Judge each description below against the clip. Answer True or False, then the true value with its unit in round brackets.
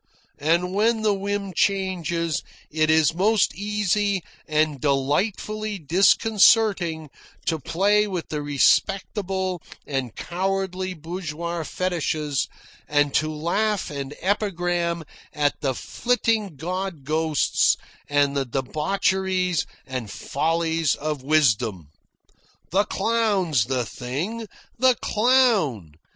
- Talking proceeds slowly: True (100 wpm)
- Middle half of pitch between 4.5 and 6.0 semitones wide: True (4.9 semitones)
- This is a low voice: False (170 Hz)